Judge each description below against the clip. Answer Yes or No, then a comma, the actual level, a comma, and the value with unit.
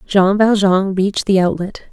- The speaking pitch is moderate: No, high, 195 Hz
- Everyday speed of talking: Yes, average, 155 wpm